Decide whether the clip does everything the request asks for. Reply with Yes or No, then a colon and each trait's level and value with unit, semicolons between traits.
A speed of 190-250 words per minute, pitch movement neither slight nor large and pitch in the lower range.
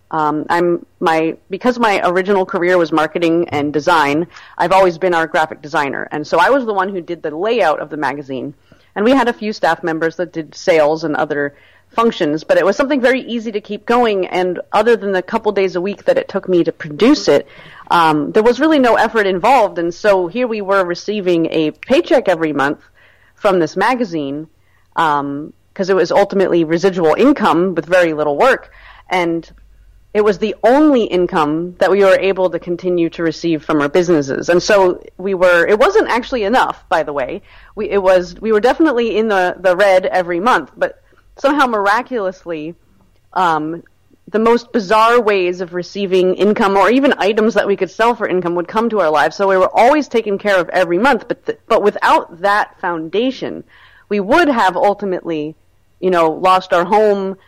No: average, 195 wpm; average, 4.3 semitones; medium, 185 Hz